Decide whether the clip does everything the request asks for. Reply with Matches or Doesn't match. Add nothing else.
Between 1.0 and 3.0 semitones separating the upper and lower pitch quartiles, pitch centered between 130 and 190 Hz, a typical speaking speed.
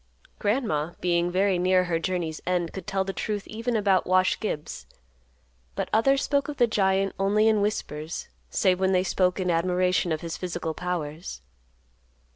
Matches